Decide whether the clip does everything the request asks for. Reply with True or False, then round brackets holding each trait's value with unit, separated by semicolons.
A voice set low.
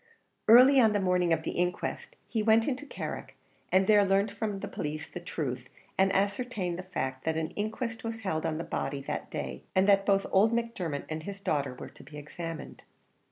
False (190 Hz)